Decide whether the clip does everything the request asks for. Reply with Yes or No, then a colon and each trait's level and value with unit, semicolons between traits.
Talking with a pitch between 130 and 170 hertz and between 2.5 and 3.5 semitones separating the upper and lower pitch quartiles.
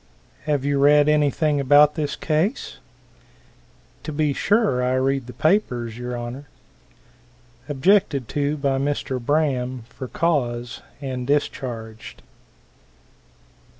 Yes: medium, 140 Hz; average, 3.1 semitones